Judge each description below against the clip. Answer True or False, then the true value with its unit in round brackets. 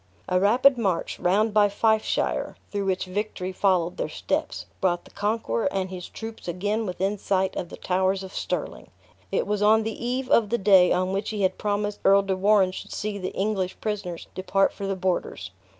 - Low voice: False (195 Hz)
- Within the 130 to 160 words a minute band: False (195 wpm)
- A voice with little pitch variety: True (2.2 semitones)